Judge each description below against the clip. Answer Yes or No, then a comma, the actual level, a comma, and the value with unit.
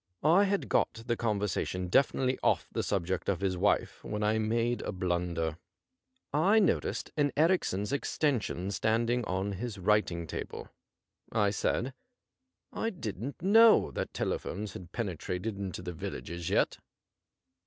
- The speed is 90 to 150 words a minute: Yes, average, 140 wpm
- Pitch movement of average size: No, wide, 6.1 semitones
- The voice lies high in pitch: No, low, 105 Hz